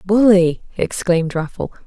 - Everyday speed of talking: No, slow, 95 wpm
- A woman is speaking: Yes, female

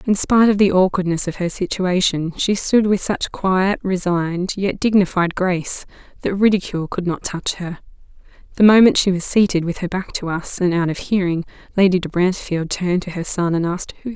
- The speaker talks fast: Yes, fast, 210 wpm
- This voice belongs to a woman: Yes, female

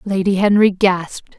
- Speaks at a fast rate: No, slow, 130 wpm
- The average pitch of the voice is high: Yes, high, 195 Hz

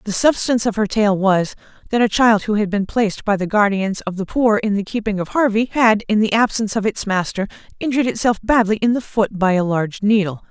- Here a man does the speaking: No, female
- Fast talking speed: Yes, fast, 235 wpm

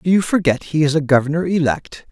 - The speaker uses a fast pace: Yes, fast, 225 wpm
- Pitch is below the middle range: No, medium, 155 Hz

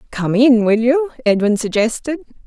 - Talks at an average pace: Yes, average, 145 wpm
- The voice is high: Yes, high, 240 Hz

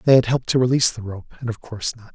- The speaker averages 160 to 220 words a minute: No, fast, 310 wpm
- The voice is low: Yes, low, 120 Hz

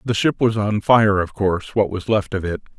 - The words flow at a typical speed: No, fast, 260 wpm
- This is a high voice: No, low, 105 Hz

